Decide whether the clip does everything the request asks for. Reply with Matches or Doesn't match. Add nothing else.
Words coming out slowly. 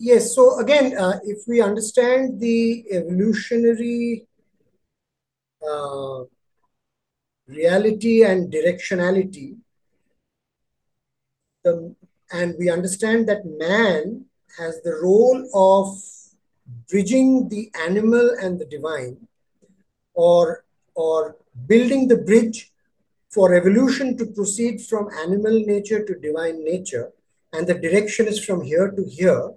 Matches